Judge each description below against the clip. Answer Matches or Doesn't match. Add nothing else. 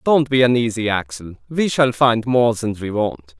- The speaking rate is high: Doesn't match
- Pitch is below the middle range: Matches